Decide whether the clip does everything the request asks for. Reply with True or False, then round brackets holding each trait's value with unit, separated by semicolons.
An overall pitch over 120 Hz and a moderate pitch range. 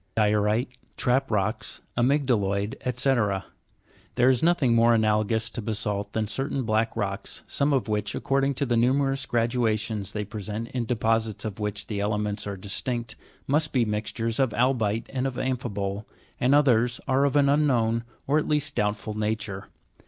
False (115 Hz; 3.6 semitones)